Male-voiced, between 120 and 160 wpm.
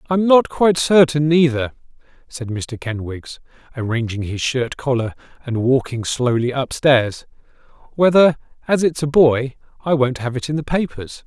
Yes: male; average, 150 wpm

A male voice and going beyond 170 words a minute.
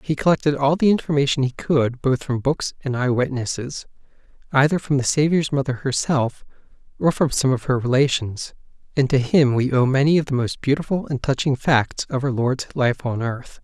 Yes: male; average, 185 wpm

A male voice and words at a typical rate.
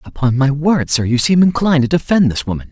No: male; fast, 245 wpm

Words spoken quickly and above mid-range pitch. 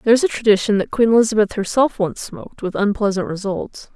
No: average, 180 wpm; high, 210 Hz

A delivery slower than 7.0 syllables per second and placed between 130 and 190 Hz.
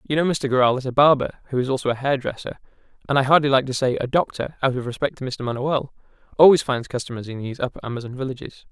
No: 7.2 syllables/s; low, 135 Hz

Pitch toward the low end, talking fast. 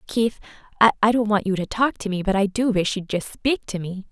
No: high, 205 Hz; fast, 265 wpm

